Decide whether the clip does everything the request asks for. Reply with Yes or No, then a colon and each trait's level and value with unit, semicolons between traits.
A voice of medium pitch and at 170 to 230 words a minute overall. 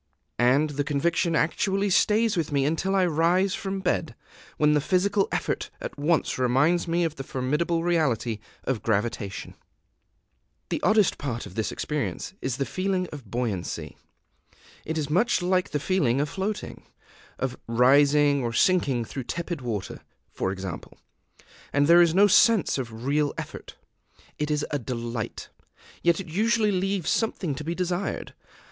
No: medium, 150 Hz; average, 155 wpm